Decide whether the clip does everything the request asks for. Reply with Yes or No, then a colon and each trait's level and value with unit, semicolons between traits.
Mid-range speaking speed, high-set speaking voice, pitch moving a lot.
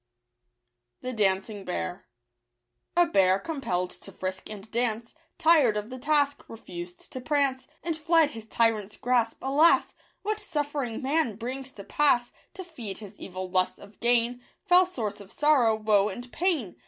Yes: average, 155 wpm; high, 235 Hz; wide, 6.5 semitones